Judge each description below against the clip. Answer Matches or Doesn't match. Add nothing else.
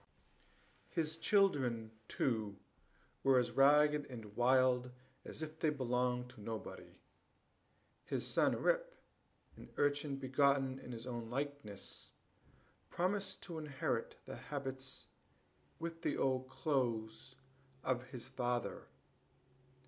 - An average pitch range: Matches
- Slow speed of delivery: Matches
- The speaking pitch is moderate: Doesn't match